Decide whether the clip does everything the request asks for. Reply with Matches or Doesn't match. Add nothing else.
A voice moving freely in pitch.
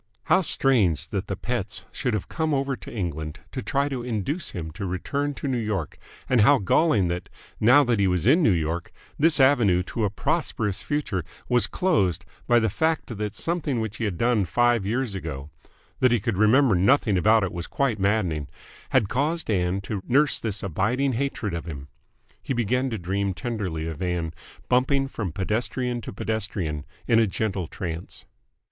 Matches